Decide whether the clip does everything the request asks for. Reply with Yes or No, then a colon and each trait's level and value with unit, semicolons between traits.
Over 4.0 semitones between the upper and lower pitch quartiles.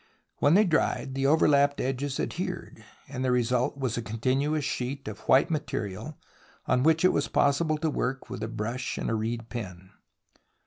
No: average, 3.5 semitones